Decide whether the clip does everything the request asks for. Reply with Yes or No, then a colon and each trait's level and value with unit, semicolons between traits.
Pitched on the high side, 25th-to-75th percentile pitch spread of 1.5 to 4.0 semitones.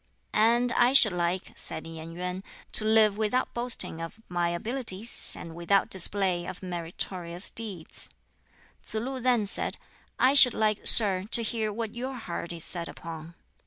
No: high, 200 Hz; average, 5.1 semitones